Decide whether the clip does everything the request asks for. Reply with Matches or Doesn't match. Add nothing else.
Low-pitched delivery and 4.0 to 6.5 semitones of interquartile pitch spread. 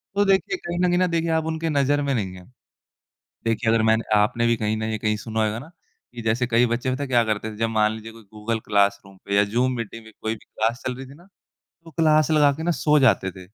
Matches